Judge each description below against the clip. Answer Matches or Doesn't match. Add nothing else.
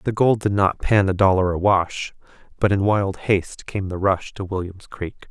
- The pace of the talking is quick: Matches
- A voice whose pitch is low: Matches